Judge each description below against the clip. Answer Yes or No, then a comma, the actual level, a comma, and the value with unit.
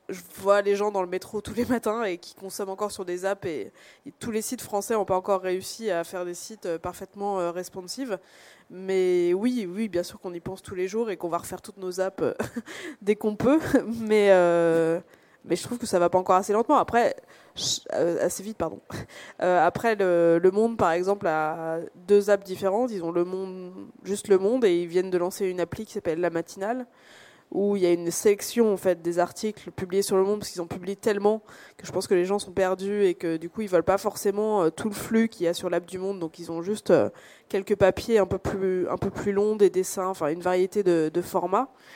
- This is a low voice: No, high, 190 Hz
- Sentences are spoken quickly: Yes, fast, 235 wpm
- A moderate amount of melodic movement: Yes, average, 3.0 semitones